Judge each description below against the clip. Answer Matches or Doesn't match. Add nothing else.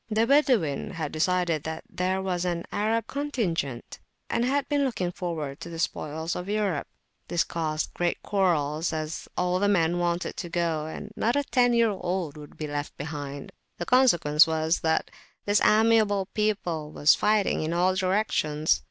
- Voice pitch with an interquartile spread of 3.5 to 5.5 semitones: Matches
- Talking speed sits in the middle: Matches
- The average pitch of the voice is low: Doesn't match